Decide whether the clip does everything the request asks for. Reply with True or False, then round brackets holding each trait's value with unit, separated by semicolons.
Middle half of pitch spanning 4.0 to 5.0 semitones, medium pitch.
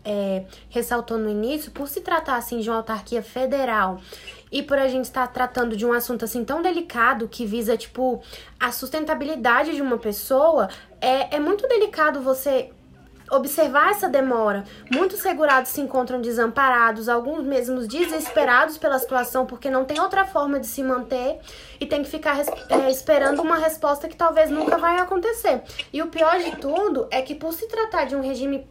False (4.3 semitones; 275 Hz)